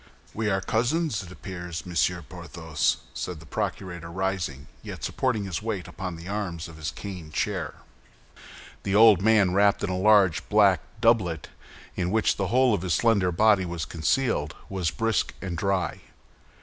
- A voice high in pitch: No, very low, 95 Hz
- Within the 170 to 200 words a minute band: No, average, 160 wpm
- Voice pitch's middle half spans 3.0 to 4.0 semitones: Yes, average, 3.5 semitones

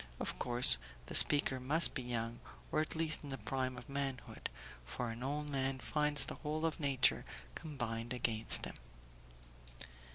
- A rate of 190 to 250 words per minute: No, average, 160 wpm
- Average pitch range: Yes, average, 3.6 semitones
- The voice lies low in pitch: Yes, low, 130 Hz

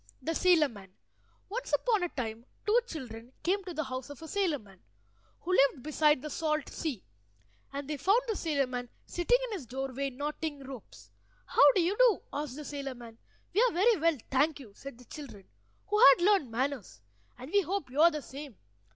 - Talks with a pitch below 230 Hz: No, very high, 290 Hz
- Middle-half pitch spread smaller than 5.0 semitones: No, wide, 5.4 semitones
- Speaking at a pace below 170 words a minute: No, average, 200 wpm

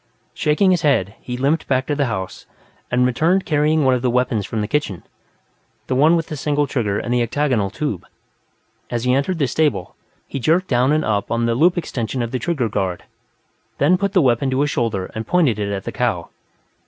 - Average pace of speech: No, fast, 215 wpm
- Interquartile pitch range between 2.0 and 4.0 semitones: No, average, 4.7 semitones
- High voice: No, low, 130 Hz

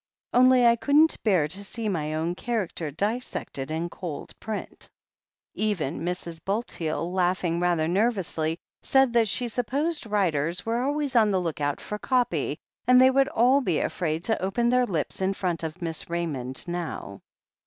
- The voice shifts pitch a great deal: Yes, wide, 6.3 semitones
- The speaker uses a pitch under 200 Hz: Yes, high, 190 Hz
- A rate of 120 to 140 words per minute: No, average, 165 wpm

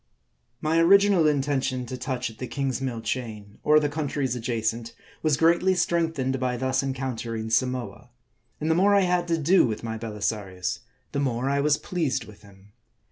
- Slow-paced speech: No, average, 170 wpm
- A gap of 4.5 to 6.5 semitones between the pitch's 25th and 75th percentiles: Yes, average, 5.1 semitones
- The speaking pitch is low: Yes, low, 130 Hz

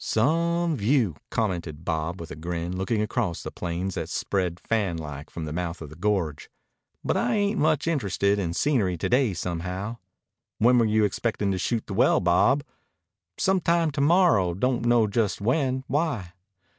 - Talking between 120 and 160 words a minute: No, average, 170 wpm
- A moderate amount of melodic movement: No, wide, 6.7 semitones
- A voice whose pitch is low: Yes, low, 105 Hz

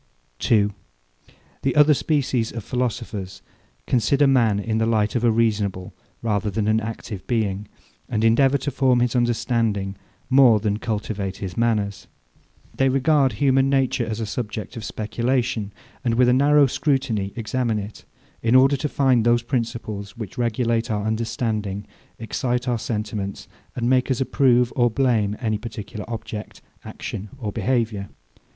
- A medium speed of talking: Yes, average, 150 wpm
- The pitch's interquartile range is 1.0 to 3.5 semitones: Yes, average, 3.1 semitones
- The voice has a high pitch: No, low, 115 Hz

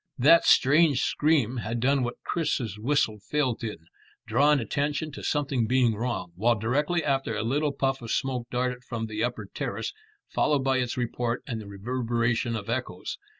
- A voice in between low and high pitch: No, low, 125 Hz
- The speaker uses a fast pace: No, average, 170 wpm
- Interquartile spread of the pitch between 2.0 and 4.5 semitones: Yes, average, 3.6 semitones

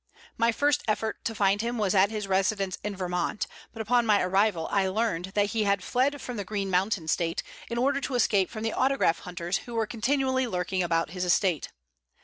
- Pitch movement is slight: No, average, 3.9 semitones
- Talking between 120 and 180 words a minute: No, fast, 205 wpm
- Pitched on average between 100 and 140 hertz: No, high, 205 Hz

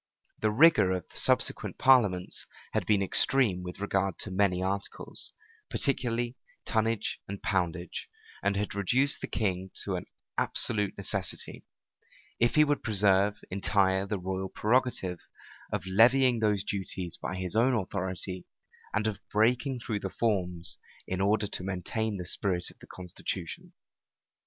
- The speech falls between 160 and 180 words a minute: No, average, 140 wpm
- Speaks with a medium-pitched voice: No, low, 100 Hz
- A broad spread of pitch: No, average, 3.1 semitones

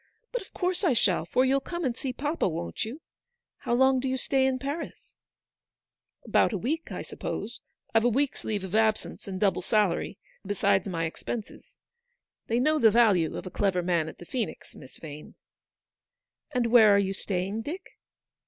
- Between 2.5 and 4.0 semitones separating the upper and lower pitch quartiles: No, wide, 5.6 semitones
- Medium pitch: No, high, 225 Hz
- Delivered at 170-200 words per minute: Yes, average, 195 wpm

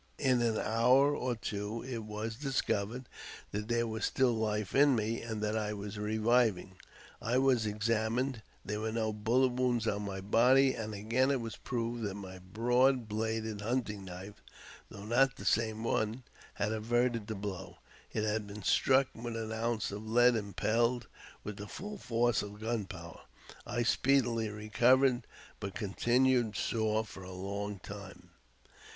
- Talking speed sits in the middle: Yes, average, 160 wpm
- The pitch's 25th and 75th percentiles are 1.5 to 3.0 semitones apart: Yes, narrow, 2.6 semitones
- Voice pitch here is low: Yes, low, 110 Hz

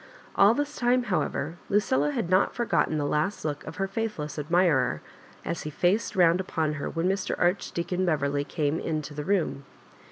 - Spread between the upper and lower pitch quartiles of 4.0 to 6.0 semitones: Yes, average, 4.4 semitones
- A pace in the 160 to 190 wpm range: Yes, average, 170 wpm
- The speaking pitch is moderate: Yes, medium, 170 Hz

